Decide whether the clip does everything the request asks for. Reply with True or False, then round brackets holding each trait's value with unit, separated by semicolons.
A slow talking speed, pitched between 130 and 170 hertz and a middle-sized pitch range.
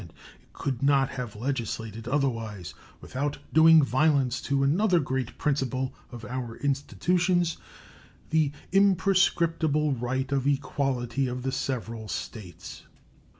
True (110 wpm; 135 Hz; 3.7 semitones)